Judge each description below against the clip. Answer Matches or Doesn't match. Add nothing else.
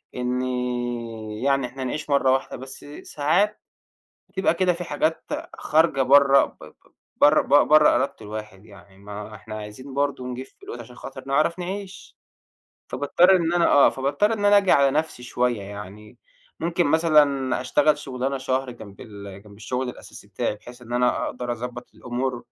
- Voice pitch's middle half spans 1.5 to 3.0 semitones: Doesn't match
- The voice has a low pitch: Matches